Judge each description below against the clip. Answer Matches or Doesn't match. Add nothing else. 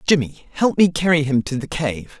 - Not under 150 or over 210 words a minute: Doesn't match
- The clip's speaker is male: Matches